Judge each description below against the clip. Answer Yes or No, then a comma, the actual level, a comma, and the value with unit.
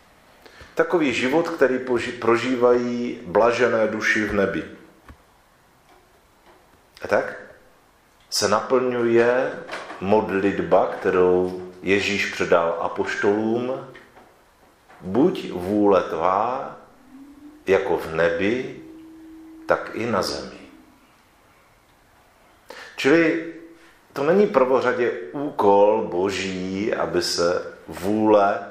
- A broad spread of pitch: Yes, wide, 8.7 semitones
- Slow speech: Yes, slow, 75 wpm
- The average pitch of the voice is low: Yes, low, 120 Hz